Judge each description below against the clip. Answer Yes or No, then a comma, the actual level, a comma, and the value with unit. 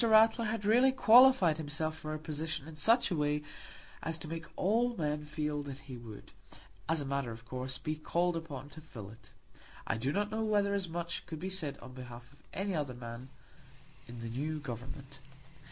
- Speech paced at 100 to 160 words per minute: No, average, 200 wpm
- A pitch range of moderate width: No, wide, 5.8 semitones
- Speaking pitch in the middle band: Yes, medium, 155 Hz